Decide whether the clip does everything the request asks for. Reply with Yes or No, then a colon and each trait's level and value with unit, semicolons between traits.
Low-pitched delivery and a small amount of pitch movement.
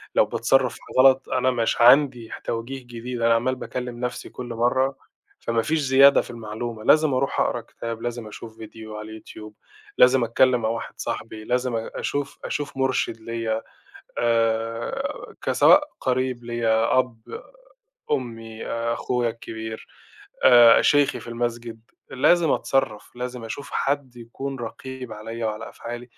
Yes: low, 120 Hz; narrow, 2.2 semitones